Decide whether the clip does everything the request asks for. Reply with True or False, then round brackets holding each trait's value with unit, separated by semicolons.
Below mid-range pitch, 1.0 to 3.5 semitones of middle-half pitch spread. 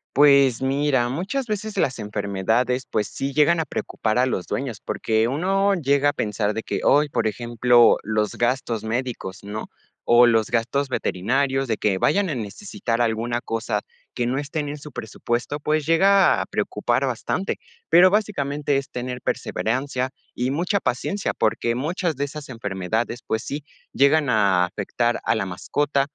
False (130 Hz; 4.7 semitones)